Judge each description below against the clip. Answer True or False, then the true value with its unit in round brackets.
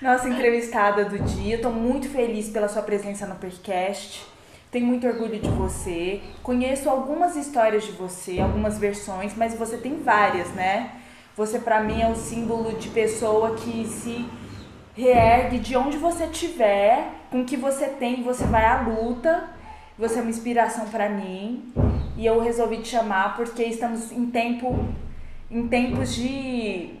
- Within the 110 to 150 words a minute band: False (160 wpm)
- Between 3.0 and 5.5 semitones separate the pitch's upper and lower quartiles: False (2.6 semitones)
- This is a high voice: True (230 Hz)